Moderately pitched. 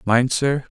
No: low, 125 Hz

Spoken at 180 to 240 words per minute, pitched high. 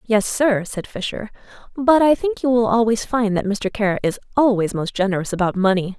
Yes: average, 200 wpm; high, 220 Hz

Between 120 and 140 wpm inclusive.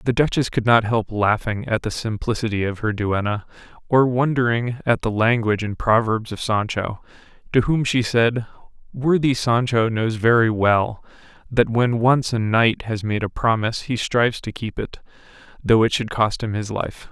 No: average, 180 wpm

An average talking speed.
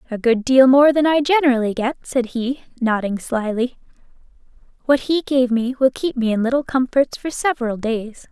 Yes: average, 180 wpm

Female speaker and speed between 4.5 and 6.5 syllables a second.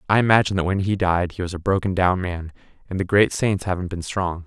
No: male; 6.1 syllables/s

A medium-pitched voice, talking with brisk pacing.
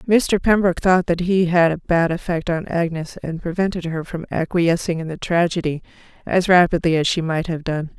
No: medium, 170 Hz; average, 195 wpm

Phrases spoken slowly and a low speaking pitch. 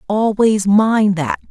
No: slow, 120 wpm; high, 205 Hz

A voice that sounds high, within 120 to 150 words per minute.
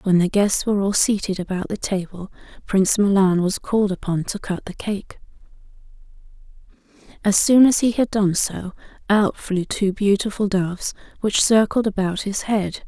No: high, 200 Hz; average, 165 wpm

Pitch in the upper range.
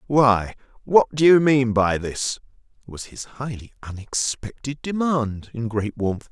No: low, 125 Hz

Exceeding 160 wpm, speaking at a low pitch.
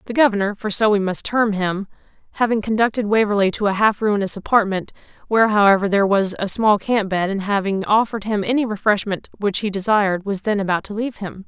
No: fast, 205 wpm; high, 205 Hz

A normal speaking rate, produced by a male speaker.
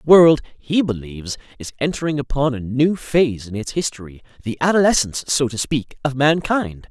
Yes: average, 175 wpm; male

